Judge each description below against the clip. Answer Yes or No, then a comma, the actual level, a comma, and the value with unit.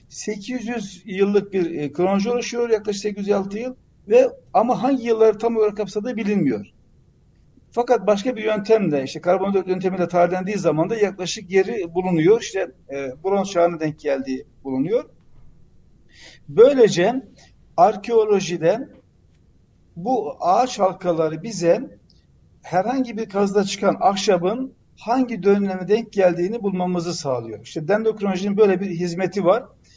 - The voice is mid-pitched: No, high, 200 Hz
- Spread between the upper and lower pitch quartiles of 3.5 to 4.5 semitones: Yes, average, 3.9 semitones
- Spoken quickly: No, average, 120 wpm